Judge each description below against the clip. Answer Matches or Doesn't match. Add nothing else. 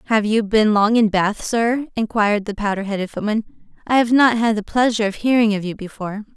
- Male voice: Doesn't match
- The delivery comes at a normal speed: Doesn't match